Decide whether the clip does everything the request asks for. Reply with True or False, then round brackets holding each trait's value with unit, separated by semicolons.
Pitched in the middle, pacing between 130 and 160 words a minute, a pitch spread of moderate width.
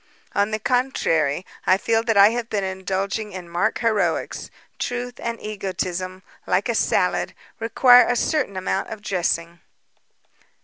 False (200 Hz; 140 wpm; 3.7 semitones)